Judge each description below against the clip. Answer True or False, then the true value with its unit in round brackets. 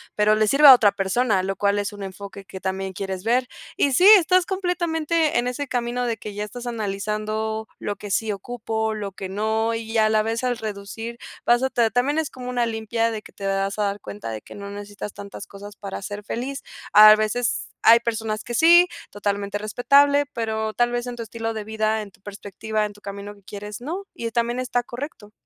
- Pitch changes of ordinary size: True (3.0 semitones)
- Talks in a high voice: True (220 Hz)